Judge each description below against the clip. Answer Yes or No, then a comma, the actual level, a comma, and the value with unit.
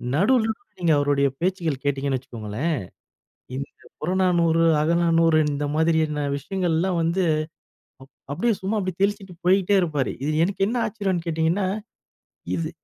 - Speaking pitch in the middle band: Yes, medium, 170 Hz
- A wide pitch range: No, average, 3.8 semitones